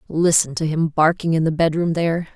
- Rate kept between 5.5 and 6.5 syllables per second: Yes, 5.7 syllables/s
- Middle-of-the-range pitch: Yes, medium, 160 Hz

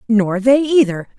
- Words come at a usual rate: Yes, average, 150 wpm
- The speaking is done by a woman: Yes, female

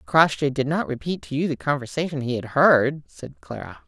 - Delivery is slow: No, average, 200 wpm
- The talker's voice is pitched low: No, medium, 145 Hz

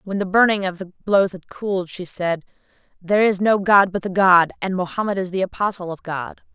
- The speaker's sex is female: Yes, female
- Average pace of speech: No, fast, 220 wpm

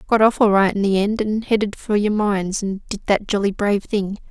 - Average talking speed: No, fast, 250 wpm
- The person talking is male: No, female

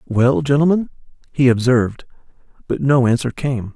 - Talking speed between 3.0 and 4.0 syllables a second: No, 5.0 syllables/s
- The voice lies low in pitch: Yes, low, 130 Hz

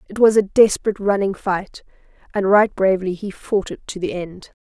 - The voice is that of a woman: Yes, female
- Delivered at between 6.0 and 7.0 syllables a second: No, 5.6 syllables/s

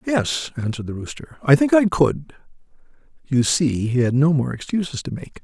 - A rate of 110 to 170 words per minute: No, average, 190 wpm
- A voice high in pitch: No, medium, 150 Hz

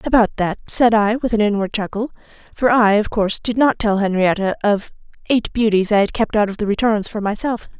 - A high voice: Yes, high, 215 Hz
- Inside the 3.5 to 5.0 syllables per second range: No, 5.6 syllables/s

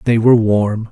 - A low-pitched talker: Yes, low, 110 Hz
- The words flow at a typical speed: Yes, average, 195 wpm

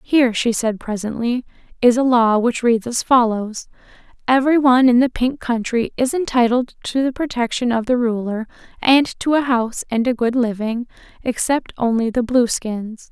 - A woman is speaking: Yes, female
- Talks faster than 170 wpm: No, average, 165 wpm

